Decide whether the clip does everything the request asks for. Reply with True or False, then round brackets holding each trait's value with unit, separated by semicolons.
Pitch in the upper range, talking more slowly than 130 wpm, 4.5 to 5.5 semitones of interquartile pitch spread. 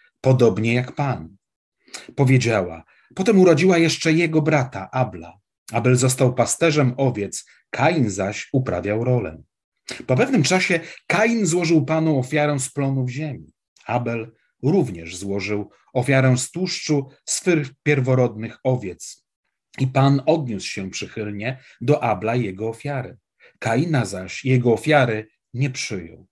False (130 Hz; 120 wpm; 4.8 semitones)